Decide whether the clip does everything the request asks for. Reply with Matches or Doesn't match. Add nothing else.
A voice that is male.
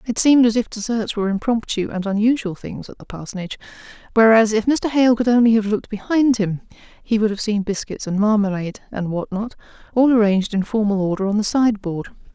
Doesn't match